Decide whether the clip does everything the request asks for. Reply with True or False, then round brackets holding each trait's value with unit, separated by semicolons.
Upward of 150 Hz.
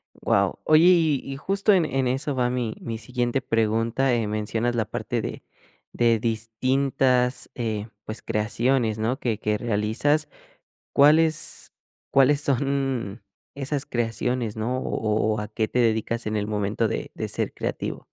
False (120 Hz)